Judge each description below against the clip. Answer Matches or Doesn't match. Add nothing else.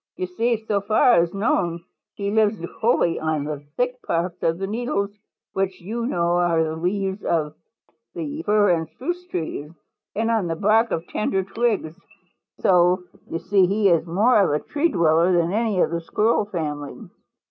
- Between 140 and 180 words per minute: Matches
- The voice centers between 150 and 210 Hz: Matches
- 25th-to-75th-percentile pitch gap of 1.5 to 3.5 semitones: Doesn't match